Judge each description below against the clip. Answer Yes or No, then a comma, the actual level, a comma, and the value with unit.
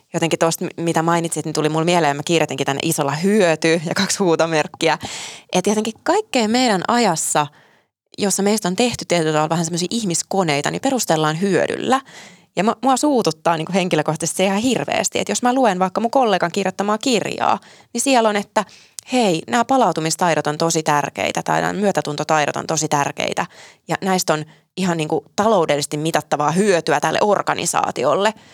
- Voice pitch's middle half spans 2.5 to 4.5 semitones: No, average, 5.0 semitones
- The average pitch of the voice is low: No, medium, 175 Hz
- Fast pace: Yes, fast, 160 wpm